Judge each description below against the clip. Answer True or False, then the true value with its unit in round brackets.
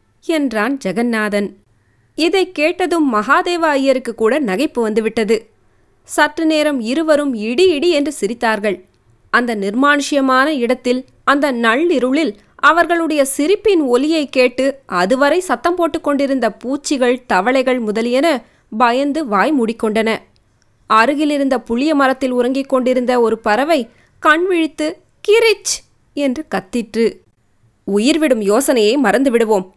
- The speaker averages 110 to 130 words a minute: False (95 wpm)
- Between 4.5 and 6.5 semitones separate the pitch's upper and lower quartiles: True (5.2 semitones)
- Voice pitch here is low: False (260 Hz)